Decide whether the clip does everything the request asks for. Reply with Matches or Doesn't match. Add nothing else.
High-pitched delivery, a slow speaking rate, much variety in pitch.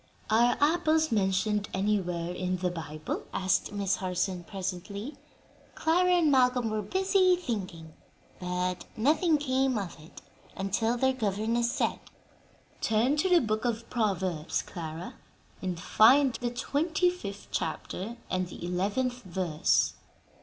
Matches